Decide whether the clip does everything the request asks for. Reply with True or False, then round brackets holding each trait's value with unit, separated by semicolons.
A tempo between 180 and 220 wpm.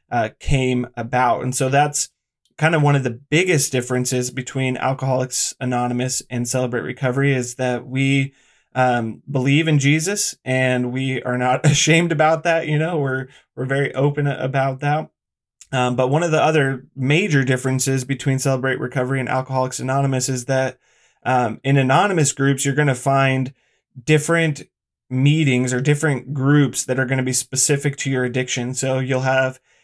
False (165 wpm)